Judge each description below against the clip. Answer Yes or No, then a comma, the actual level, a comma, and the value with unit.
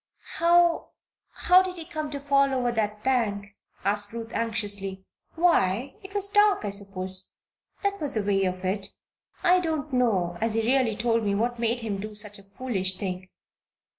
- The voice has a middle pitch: No, high, 225 Hz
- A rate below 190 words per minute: Yes, average, 175 wpm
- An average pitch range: No, wide, 6.0 semitones